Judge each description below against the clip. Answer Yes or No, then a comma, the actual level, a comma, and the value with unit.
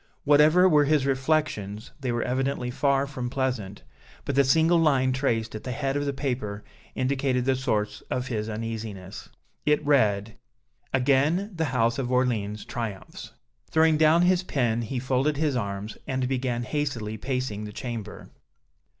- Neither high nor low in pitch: No, low, 130 Hz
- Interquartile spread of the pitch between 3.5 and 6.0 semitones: Yes, average, 3.9 semitones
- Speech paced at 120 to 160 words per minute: Yes, average, 155 wpm